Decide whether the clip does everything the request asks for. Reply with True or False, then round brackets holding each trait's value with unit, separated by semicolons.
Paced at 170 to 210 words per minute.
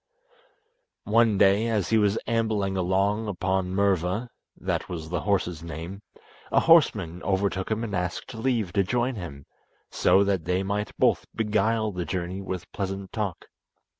False (150 wpm)